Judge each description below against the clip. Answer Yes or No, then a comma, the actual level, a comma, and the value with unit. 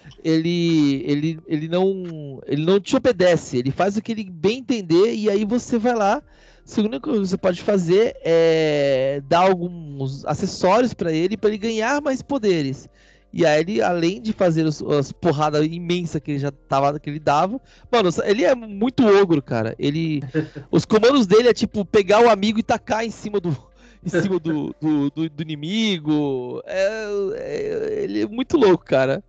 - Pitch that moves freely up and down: Yes, wide, 6.3 semitones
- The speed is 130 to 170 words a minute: No, average, 180 wpm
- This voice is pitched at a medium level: Yes, medium, 180 Hz